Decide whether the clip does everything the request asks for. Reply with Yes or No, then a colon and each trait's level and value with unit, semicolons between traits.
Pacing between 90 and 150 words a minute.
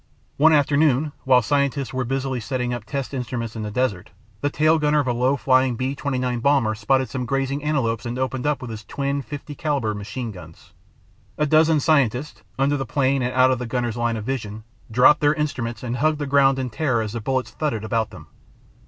No: fast, 205 wpm